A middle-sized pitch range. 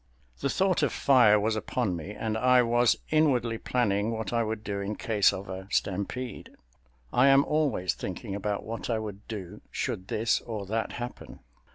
Yes: average, 3.3 semitones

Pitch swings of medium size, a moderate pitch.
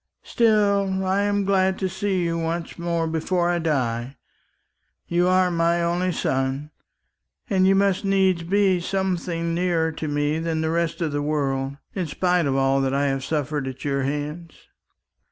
Yes: average, 4.1 semitones; medium, 170 Hz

